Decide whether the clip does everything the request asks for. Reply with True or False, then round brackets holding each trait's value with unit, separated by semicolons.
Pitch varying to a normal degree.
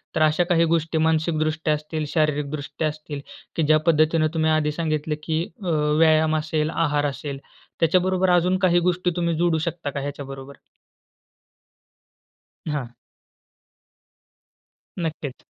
False (1.8 semitones)